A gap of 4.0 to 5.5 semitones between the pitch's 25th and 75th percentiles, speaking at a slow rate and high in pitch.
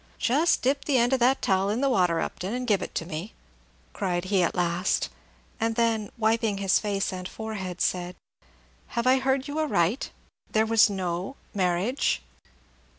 No: average, 5.1 semitones; average, 170 wpm; high, 210 Hz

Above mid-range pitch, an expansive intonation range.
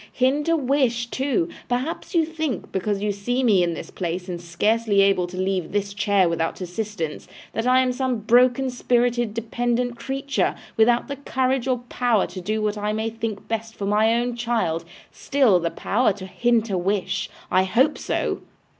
No: high, 225 Hz; average, 4.0 semitones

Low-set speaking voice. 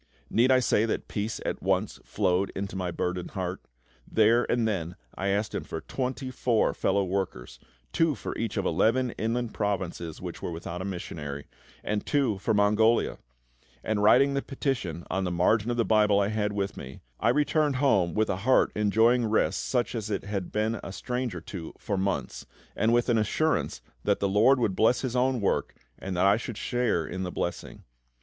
Yes: low, 105 Hz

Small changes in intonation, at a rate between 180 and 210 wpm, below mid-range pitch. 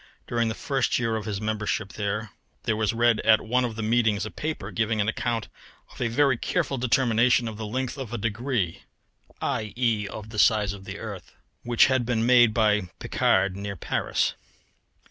Yes: narrow, 2.3 semitones; average, 185 wpm; low, 110 Hz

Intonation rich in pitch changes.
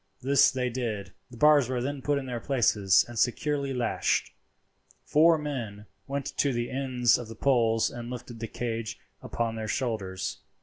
No: average, 3.3 semitones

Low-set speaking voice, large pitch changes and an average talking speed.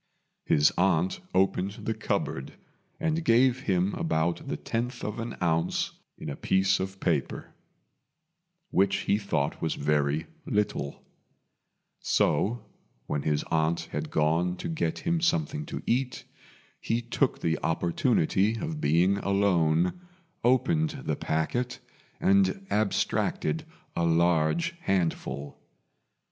No: very low, 95 Hz; wide, 7.4 semitones; slow, 120 wpm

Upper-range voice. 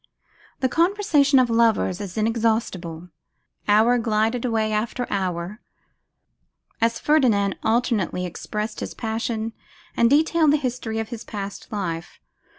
Yes: high, 225 Hz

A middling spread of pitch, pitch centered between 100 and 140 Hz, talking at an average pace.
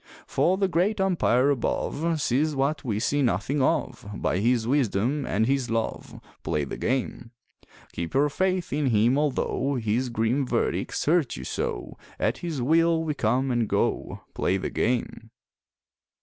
Yes: average, 4.8 semitones; low, 135 Hz; average, 155 wpm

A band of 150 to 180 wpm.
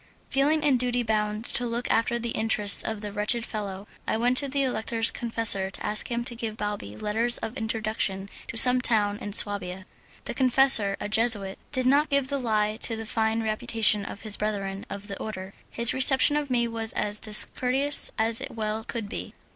No: average, 195 wpm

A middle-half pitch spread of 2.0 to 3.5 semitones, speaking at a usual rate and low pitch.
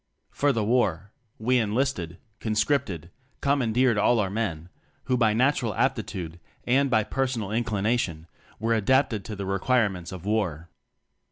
No: average, 4.4 semitones; average, 150 wpm; low, 110 Hz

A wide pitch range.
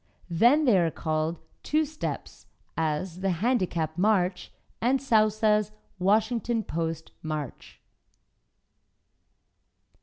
Yes: wide, 5.7 semitones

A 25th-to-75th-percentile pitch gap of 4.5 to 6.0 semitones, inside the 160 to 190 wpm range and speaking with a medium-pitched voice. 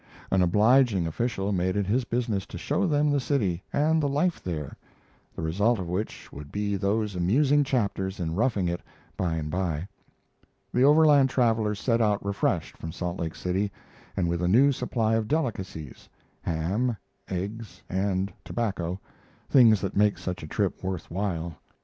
No: average, 5.0 semitones; average, 165 wpm; low, 100 Hz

